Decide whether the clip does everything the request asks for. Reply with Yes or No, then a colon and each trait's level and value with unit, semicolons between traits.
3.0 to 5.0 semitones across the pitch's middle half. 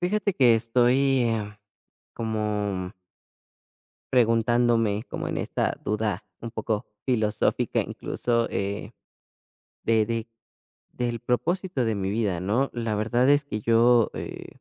No: narrow, 2.4 semitones